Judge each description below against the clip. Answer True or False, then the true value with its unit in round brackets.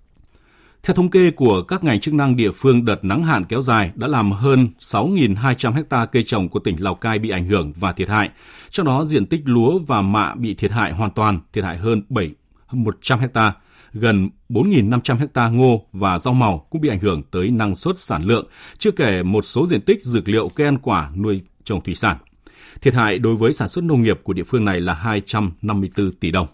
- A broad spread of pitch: False (4.6 semitones)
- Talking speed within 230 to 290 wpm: False (215 wpm)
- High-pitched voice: False (110 Hz)